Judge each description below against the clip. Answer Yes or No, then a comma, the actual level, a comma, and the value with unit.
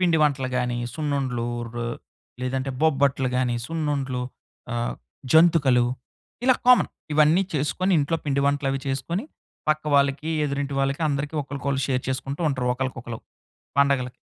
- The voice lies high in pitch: No, medium, 140 Hz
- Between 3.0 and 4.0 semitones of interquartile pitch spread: No, narrow, 2.6 semitones